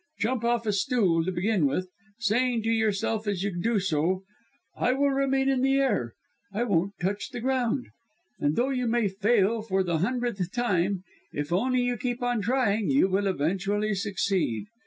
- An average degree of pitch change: Yes, average, 4.4 semitones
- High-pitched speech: Yes, high, 215 Hz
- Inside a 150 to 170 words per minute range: No, average, 180 wpm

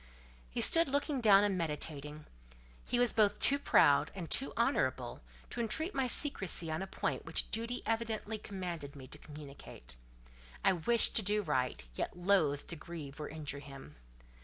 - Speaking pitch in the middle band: Yes, medium, 180 Hz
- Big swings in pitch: Yes, wide, 7.2 semitones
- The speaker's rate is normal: Yes, average, 165 wpm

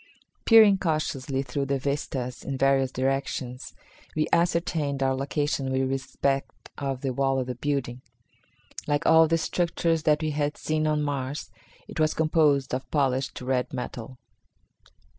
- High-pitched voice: No, medium, 140 Hz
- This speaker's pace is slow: No, average, 145 wpm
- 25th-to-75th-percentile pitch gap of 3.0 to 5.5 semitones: No, narrow, 2.6 semitones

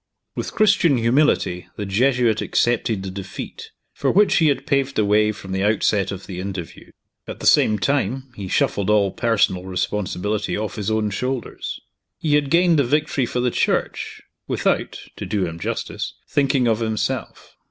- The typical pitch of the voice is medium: No, low, 110 Hz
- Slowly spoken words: No, average, 170 wpm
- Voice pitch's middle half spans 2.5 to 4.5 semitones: No, wide, 5.4 semitones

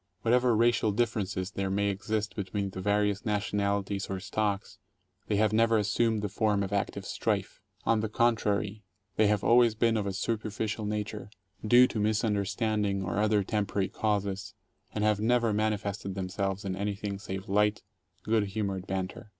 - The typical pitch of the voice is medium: No, low, 105 Hz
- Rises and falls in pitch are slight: Yes, narrow, 1.7 semitones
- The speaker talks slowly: No, average, 165 wpm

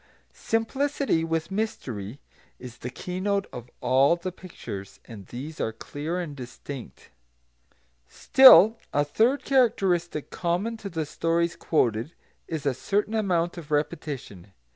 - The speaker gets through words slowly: Yes, slow, 125 wpm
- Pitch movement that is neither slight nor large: No, wide, 7.1 semitones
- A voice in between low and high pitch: Yes, medium, 165 Hz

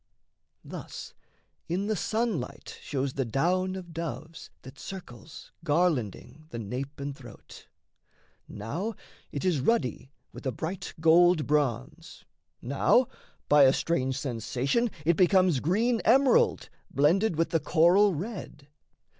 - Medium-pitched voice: Yes, medium, 160 Hz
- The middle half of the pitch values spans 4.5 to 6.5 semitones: Yes, wide, 5.4 semitones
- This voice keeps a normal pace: No, slow, 120 wpm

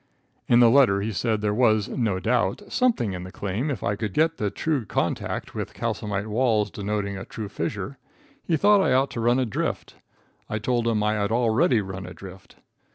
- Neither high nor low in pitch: No, low, 110 Hz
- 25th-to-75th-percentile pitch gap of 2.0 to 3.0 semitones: No, average, 3.6 semitones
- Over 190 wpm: Yes, average, 200 wpm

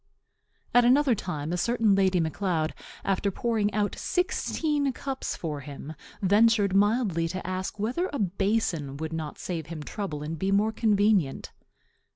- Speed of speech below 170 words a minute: Yes, average, 155 wpm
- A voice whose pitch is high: Yes, high, 195 Hz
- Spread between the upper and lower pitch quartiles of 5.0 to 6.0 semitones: Yes, wide, 5.4 semitones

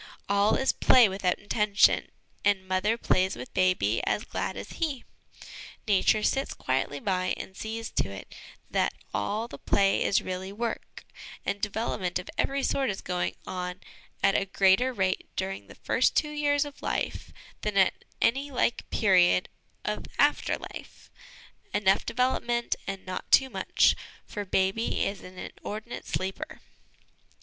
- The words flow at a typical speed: Yes, average, 150 wpm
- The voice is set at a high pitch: Yes, high, 200 Hz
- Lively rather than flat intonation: No, average, 3.8 semitones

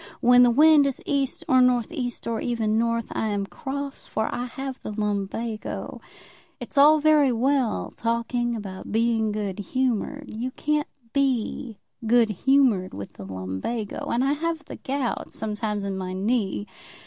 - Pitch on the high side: Yes, high, 235 Hz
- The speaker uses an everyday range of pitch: Yes, average, 4.2 semitones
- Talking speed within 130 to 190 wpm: Yes, average, 160 wpm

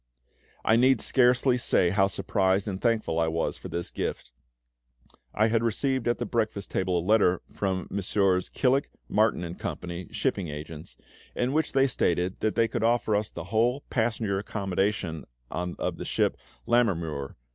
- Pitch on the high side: No, low, 100 Hz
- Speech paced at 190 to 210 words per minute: No, average, 160 wpm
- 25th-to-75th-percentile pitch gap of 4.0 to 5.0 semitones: Yes, average, 4.7 semitones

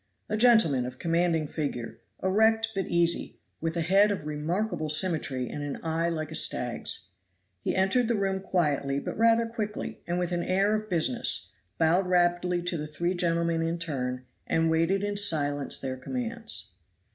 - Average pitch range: Yes, average, 4.2 semitones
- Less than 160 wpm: No, average, 170 wpm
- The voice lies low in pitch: No, medium, 170 Hz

